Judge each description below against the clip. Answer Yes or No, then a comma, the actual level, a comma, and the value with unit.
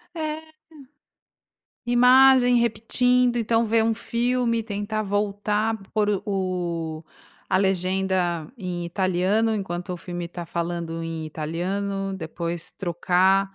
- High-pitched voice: Yes, high, 195 Hz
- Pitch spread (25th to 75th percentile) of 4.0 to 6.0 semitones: Yes, average, 4.5 semitones